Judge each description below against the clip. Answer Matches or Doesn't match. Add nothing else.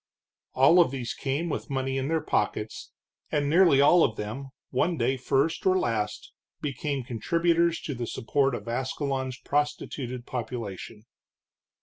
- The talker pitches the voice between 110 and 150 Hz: Matches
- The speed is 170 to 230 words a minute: Doesn't match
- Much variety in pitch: Doesn't match